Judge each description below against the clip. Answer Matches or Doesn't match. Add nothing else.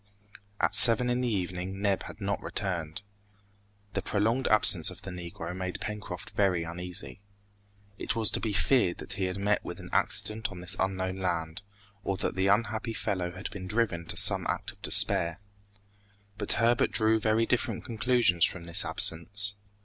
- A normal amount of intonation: Matches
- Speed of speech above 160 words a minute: Matches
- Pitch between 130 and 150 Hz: Doesn't match